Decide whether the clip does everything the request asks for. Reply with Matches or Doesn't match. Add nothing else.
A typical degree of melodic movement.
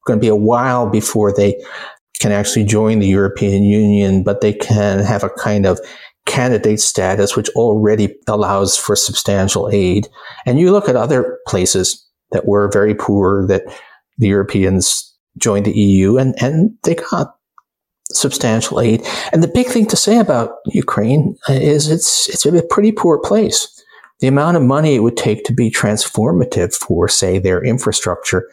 Matches